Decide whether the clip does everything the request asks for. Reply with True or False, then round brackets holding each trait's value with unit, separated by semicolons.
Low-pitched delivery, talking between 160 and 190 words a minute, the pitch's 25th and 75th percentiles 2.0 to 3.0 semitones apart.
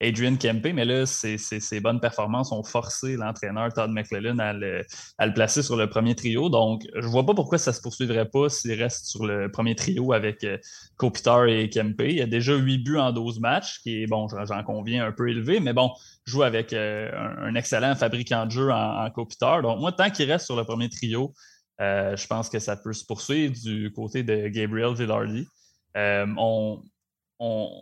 False (115 Hz; 215 wpm; 2.6 semitones)